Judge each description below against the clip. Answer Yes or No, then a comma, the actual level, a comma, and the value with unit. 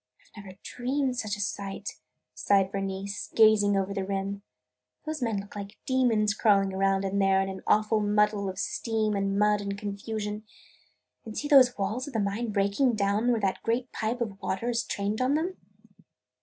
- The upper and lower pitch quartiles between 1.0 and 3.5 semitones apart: Yes, narrow, 2.6 semitones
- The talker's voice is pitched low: No, high, 210 Hz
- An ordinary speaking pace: Yes, average, 185 wpm